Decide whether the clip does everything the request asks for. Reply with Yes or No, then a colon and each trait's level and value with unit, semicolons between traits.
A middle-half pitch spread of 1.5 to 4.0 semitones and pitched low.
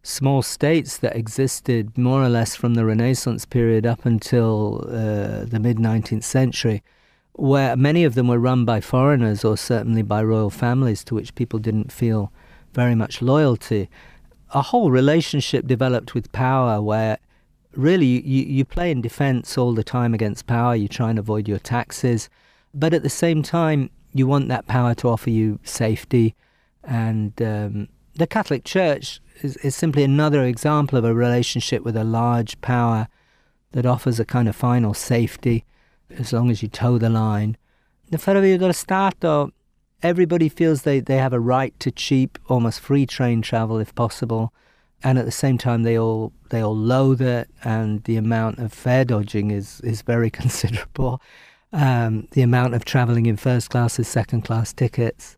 Yes: average, 3.0 semitones; low, 120 Hz